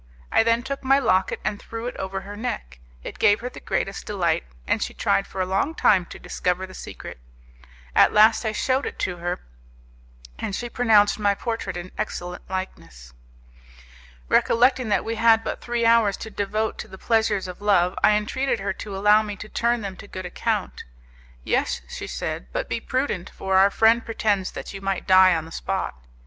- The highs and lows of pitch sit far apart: No, average, 3.3 semitones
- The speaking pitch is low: No, high, 205 Hz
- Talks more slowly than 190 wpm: No, average, 195 wpm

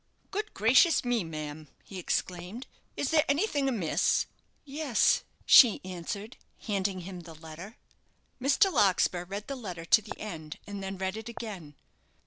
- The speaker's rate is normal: Yes, average, 145 wpm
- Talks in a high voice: Yes, high, 200 Hz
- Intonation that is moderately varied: No, wide, 5.7 semitones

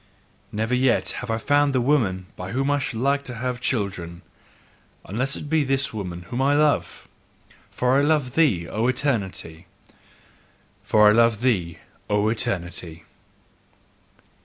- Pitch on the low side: Yes, low, 120 Hz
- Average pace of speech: Yes, average, 145 wpm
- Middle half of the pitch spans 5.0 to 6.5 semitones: Yes, wide, 5.5 semitones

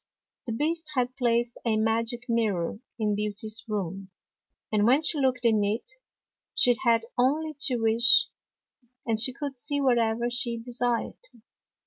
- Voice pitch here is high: Yes, high, 235 Hz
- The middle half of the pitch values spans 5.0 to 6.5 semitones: No, narrow, 2.4 semitones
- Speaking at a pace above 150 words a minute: No, average, 145 wpm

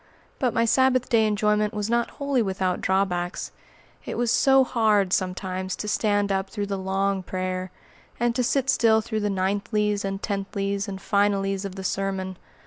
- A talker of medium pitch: No, high, 200 Hz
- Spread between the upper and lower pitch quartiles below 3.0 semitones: Yes, narrow, 2.4 semitones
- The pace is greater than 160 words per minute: Yes, average, 170 wpm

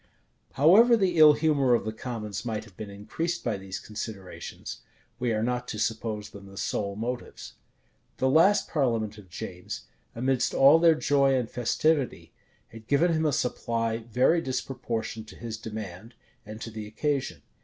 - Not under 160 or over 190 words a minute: Yes, average, 165 wpm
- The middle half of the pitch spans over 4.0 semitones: Yes, average, 4.6 semitones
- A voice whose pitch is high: No, low, 120 Hz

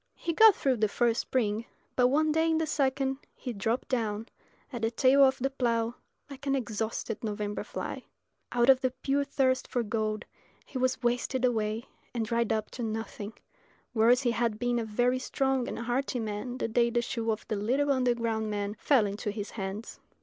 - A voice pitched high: Yes, high, 240 Hz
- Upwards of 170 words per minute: Yes, average, 195 wpm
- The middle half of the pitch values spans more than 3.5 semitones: No, average, 3.0 semitones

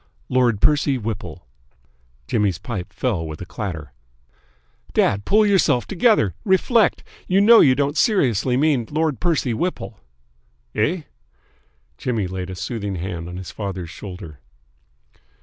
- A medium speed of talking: No, slow, 130 wpm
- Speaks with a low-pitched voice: Yes, low, 115 Hz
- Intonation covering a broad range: Yes, wide, 8.5 semitones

